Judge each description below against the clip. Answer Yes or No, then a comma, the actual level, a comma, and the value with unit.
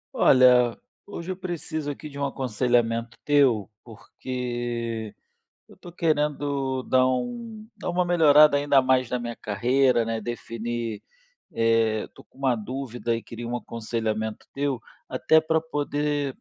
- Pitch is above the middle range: No, low, 130 Hz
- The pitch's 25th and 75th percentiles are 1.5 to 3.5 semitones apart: No, average, 3.9 semitones